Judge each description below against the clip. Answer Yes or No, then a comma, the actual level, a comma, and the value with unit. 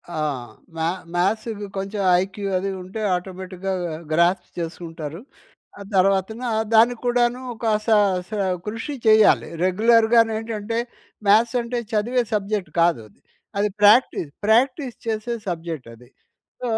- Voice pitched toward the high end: Yes, high, 210 Hz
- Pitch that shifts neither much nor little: Yes, average, 4.1 semitones